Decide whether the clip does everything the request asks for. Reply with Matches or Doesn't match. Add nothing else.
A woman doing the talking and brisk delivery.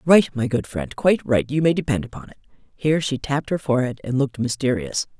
Matches